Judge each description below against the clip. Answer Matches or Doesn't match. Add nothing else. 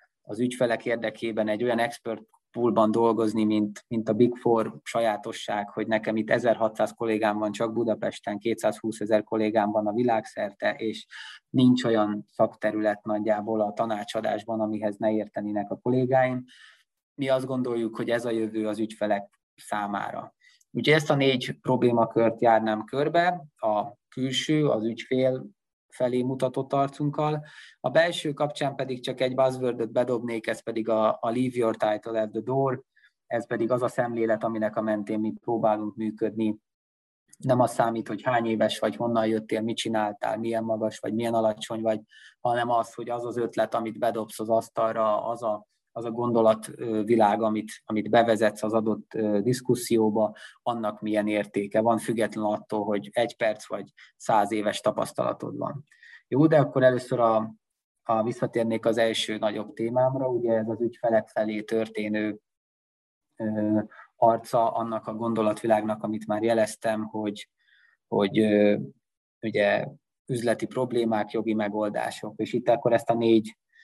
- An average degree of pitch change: Doesn't match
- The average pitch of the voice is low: Matches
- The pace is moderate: Matches